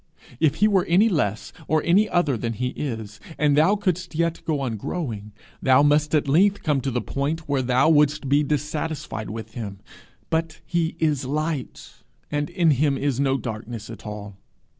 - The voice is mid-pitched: Yes, medium, 145 Hz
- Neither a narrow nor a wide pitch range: Yes, average, 4.6 semitones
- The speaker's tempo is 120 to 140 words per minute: No, average, 180 wpm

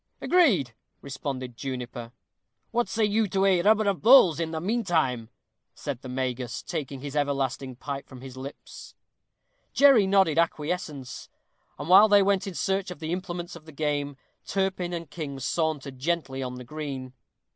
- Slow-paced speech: No, average, 165 wpm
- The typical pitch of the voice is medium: Yes, medium, 155 Hz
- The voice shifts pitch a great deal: Yes, wide, 6.2 semitones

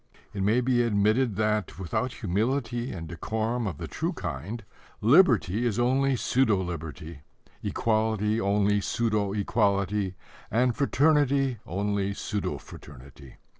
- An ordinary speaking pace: No, slow, 120 wpm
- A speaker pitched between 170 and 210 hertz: No, low, 105 Hz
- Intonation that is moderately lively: Yes, average, 3.7 semitones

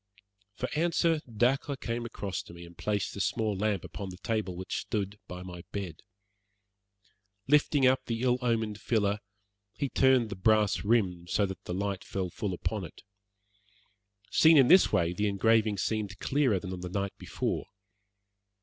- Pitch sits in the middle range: No, low, 105 Hz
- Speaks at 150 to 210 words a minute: Yes, average, 170 wpm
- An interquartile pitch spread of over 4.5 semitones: No, average, 4.1 semitones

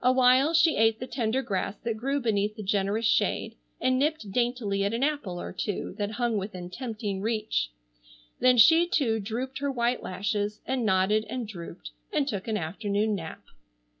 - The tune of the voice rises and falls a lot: No, average, 3.9 semitones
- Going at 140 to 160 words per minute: No, average, 175 wpm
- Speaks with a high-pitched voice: Yes, high, 220 Hz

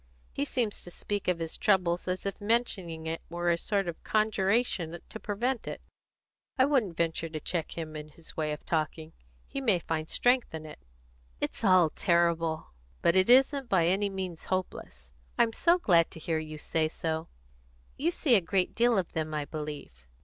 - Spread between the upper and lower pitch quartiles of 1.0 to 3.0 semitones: No, average, 4.5 semitones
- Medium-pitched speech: Yes, medium, 175 Hz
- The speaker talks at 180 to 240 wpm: Yes, average, 185 wpm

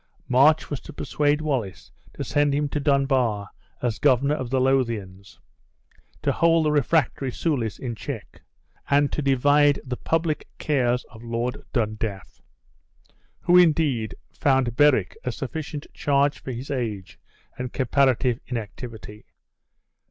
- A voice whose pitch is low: Yes, low, 130 Hz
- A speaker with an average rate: No, slow, 130 wpm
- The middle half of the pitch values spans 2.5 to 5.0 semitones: Yes, average, 3.8 semitones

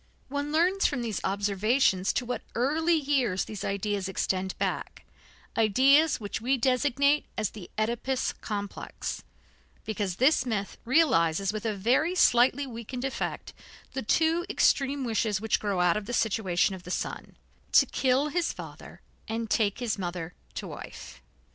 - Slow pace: No, average, 150 wpm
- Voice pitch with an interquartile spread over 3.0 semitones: Yes, average, 5.3 semitones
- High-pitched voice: Yes, high, 230 Hz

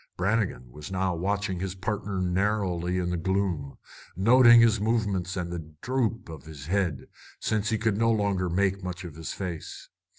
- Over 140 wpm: Yes, average, 170 wpm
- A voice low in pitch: Yes, very low, 95 Hz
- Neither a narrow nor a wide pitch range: Yes, average, 3.2 semitones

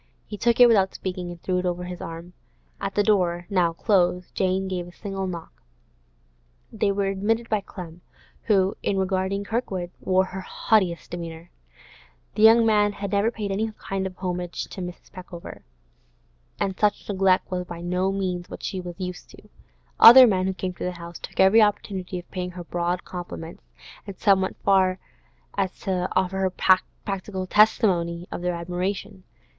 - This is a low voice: No, medium, 185 Hz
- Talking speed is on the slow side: No, average, 175 wpm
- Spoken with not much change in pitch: Yes, narrow, 2.0 semitones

